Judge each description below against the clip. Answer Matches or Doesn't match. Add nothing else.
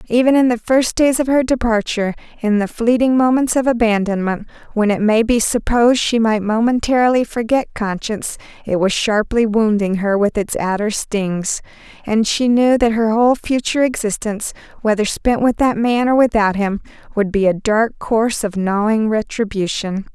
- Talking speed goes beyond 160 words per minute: Matches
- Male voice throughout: Doesn't match